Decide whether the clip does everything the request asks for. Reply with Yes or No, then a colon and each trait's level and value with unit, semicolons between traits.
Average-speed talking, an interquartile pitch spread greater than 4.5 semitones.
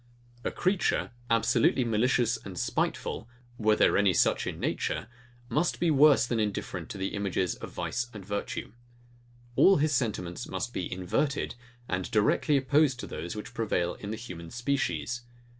Yes: average, 160 wpm; average, 5.1 semitones